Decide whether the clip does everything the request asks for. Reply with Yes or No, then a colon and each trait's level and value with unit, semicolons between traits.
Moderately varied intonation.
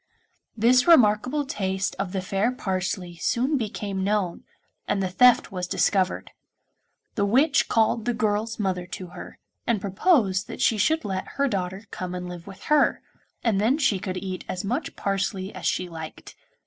Yes: average, 4.0 semitones